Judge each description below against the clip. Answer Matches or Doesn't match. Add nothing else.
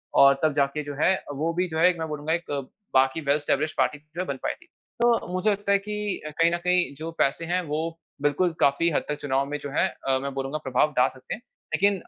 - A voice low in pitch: Doesn't match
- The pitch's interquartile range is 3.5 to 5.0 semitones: Matches